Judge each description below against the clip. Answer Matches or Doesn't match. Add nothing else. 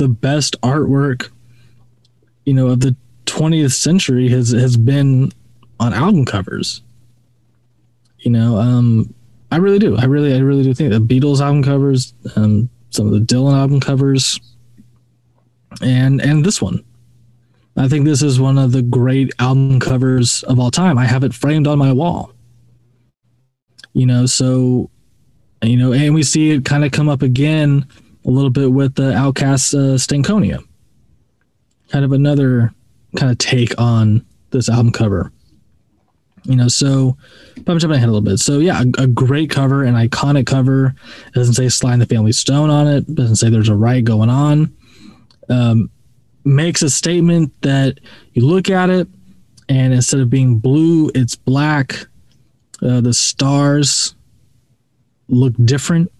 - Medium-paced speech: Matches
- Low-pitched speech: Matches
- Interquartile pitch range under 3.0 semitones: Matches